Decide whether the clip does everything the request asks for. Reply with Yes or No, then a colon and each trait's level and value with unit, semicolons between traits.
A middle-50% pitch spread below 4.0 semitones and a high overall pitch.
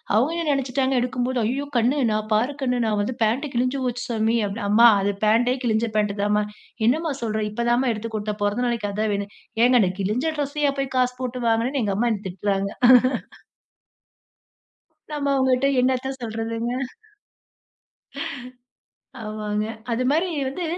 Yes: average, 3.3 semitones; high, 235 Hz